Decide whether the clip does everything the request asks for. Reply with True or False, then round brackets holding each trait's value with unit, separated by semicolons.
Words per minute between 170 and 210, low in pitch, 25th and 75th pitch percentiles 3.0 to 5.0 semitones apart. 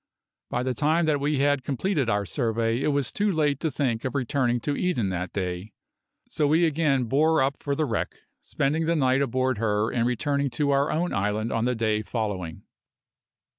True (195 wpm; 130 Hz; 4.5 semitones)